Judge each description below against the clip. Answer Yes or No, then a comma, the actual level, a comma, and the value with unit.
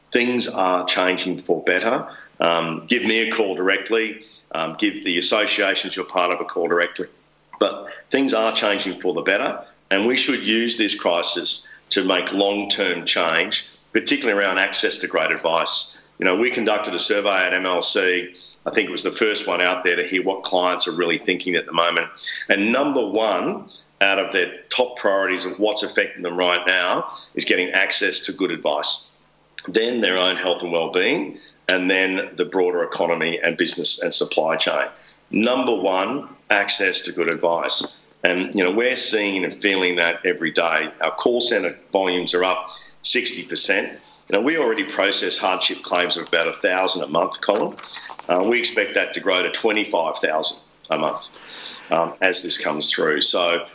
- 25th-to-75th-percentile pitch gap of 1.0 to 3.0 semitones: No, average, 3.7 semitones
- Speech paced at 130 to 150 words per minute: No, average, 180 wpm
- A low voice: Yes, very low, 95 Hz